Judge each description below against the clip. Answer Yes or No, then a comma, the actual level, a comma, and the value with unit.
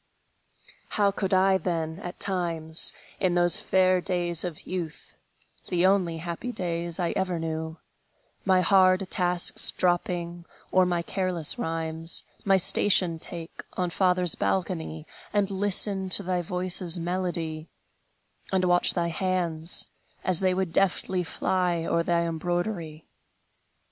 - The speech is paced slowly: Yes, slow, 130 wpm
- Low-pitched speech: No, medium, 175 Hz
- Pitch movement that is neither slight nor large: No, narrow, 1.9 semitones